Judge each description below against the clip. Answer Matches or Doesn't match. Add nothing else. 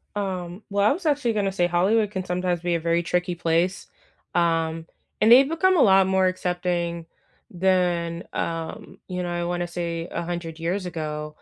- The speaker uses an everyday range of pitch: Doesn't match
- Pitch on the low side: Doesn't match